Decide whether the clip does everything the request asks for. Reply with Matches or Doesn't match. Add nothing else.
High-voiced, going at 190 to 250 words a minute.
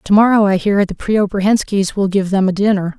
Matches